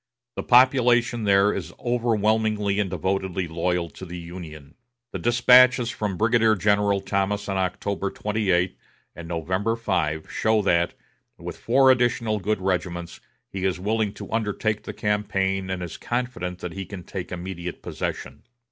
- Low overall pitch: Yes, low, 100 Hz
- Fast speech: No, average, 145 wpm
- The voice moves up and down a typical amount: Yes, average, 3.4 semitones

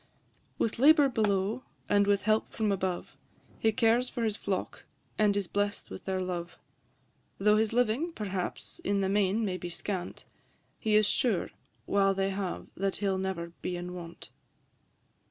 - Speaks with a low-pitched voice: No, high, 200 Hz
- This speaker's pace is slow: No, average, 165 wpm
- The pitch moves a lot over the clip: No, narrow, 2.5 semitones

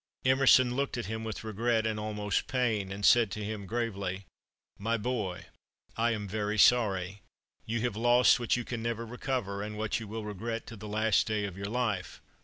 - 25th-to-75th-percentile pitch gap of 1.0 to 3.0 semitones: Yes, narrow, 2.4 semitones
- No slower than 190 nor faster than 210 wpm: Yes, average, 195 wpm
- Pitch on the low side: Yes, low, 110 Hz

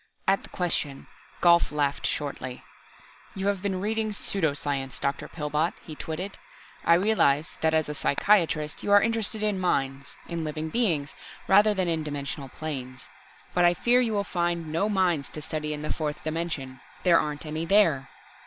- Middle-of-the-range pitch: Yes, medium, 160 Hz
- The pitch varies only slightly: No, average, 4.6 semitones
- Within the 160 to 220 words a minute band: Yes, average, 170 wpm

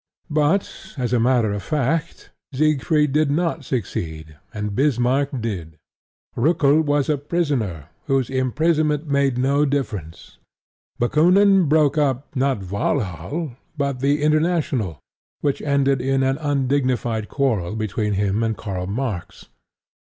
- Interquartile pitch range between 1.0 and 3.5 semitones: No, average, 5.1 semitones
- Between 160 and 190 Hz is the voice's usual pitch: No, low, 135 Hz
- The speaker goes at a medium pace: No, slow, 125 wpm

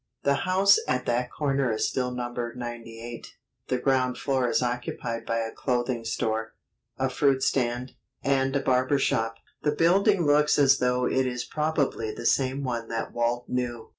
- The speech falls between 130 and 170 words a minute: Yes, average, 165 wpm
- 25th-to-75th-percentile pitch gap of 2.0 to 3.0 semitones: Yes, narrow, 2.5 semitones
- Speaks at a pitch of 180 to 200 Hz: No, low, 125 Hz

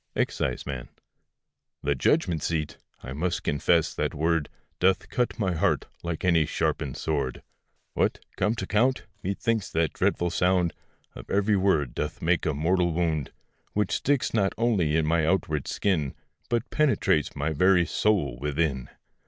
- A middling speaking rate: Yes, average, 145 wpm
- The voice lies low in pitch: Yes, very low, 85 Hz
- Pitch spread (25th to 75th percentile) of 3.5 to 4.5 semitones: Yes, average, 4.2 semitones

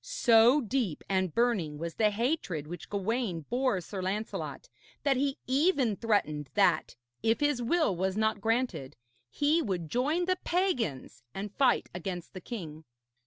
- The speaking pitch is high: Yes, high, 220 Hz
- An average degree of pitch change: No, wide, 6.3 semitones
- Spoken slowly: No, average, 150 wpm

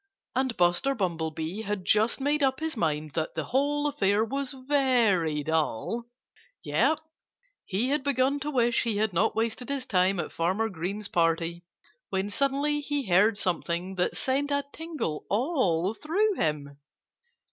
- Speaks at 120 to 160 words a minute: Yes, average, 150 wpm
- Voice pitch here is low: No, high, 220 Hz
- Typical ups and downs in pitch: No, wide, 7.9 semitones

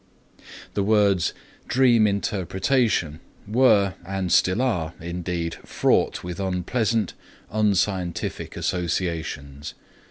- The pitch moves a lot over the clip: No, average, 3.8 semitones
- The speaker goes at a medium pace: No, slow, 85 wpm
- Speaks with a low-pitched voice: Yes, very low, 95 Hz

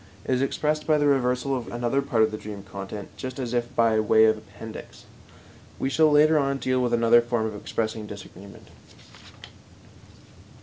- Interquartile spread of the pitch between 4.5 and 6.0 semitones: No, average, 3.8 semitones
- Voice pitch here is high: No, low, 120 Hz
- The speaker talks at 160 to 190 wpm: Yes, average, 175 wpm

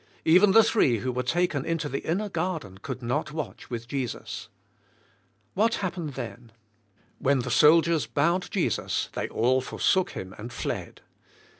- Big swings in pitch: Yes, wide, 5.8 semitones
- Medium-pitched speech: Yes, medium, 150 Hz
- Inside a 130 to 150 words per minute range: No, average, 160 wpm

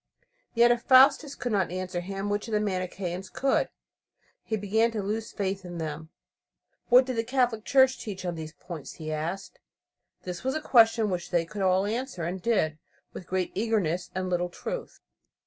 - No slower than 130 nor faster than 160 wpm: No, average, 180 wpm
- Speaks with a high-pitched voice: Yes, high, 195 Hz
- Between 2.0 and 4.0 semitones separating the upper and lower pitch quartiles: No, average, 4.5 semitones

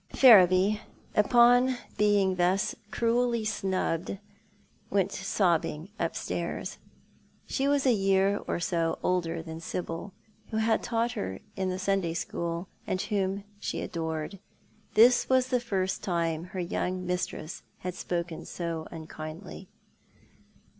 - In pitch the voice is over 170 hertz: Yes, medium, 185 Hz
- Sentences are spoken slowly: Yes, slow, 120 wpm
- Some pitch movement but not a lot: Yes, average, 3.9 semitones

